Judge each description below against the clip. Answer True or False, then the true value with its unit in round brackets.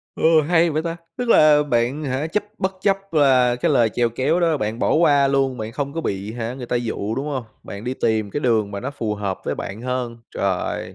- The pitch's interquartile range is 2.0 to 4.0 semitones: False (5.0 semitones)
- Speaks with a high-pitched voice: False (130 Hz)